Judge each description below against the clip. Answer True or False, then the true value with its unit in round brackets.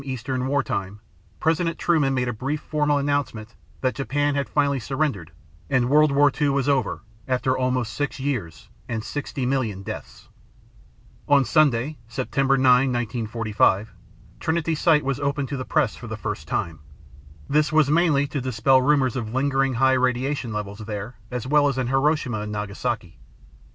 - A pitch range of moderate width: True (3.5 semitones)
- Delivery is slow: False (160 wpm)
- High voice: False (130 Hz)